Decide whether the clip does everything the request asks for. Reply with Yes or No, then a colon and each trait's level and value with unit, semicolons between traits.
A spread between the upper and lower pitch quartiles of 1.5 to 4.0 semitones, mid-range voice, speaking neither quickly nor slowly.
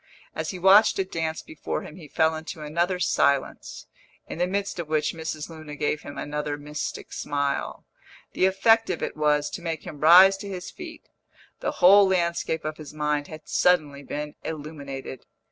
Yes: average, 3.4 semitones; medium, 160 Hz; average, 180 wpm